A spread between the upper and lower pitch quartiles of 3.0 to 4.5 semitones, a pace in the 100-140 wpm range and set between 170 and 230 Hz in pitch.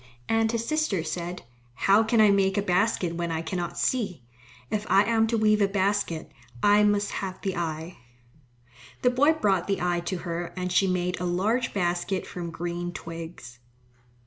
No: average, 3.3 semitones; average, 175 wpm; high, 190 Hz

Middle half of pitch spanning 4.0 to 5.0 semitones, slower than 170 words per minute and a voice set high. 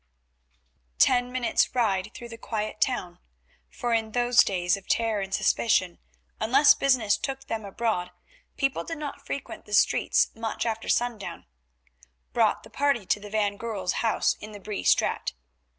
No: average, 3.1 semitones; average, 155 wpm; high, 225 Hz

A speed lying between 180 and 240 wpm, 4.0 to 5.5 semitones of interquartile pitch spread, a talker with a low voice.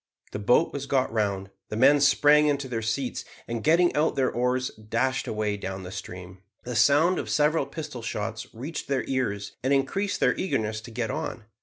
Yes: average, 190 wpm; average, 4.7 semitones; low, 125 Hz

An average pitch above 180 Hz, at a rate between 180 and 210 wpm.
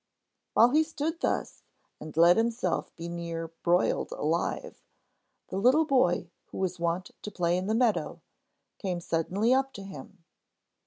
No: high, 190 Hz; average, 150 wpm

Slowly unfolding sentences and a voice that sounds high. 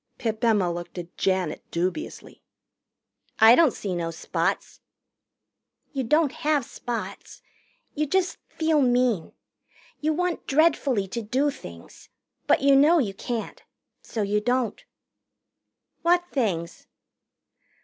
Yes: slow, 120 wpm; high, 245 Hz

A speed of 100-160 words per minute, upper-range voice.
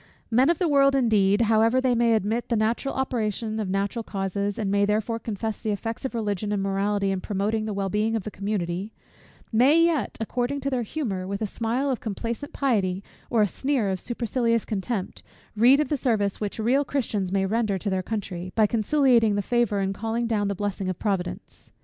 No: fast, 205 wpm; high, 220 Hz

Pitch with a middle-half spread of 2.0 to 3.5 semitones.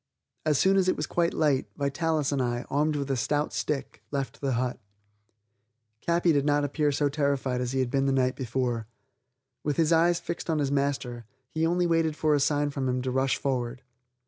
Yes: average, 2.8 semitones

